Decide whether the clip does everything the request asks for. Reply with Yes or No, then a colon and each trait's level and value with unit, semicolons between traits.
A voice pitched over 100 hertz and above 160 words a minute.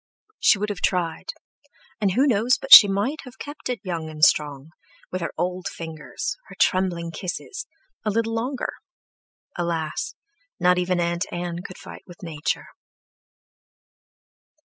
No: medium, 185 Hz; average, 140 wpm